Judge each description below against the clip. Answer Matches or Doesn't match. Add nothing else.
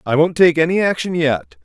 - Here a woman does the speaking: Doesn't match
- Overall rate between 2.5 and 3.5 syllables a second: Doesn't match